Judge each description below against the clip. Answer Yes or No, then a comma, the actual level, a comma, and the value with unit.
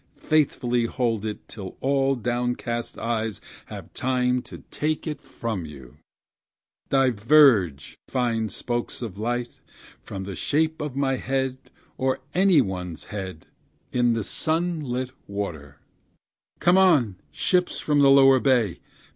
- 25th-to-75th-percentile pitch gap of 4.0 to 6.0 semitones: Yes, average, 4.4 semitones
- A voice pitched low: Yes, low, 125 Hz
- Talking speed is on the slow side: Yes, slow, 130 wpm